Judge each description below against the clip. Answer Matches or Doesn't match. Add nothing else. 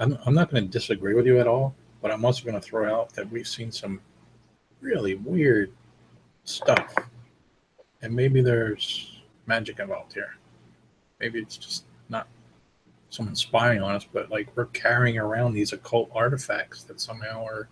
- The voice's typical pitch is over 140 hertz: Doesn't match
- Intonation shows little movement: Matches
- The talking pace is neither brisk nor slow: Matches